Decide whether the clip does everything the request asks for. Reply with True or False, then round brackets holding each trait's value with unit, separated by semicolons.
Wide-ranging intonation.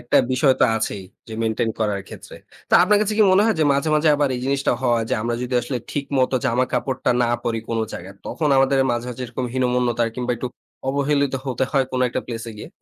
False (2.8 semitones)